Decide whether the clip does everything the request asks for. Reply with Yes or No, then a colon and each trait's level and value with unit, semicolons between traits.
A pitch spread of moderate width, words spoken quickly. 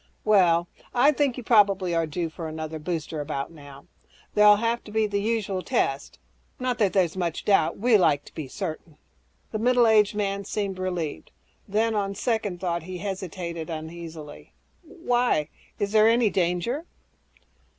No: average, 4.7 semitones; average, 160 wpm